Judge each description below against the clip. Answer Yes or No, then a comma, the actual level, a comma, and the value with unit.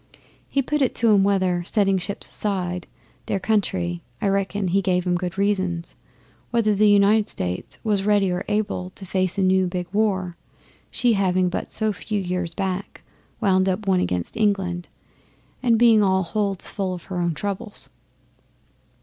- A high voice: Yes, high, 195 Hz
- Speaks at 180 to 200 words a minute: No, average, 165 wpm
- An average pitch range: No, narrow, 2.3 semitones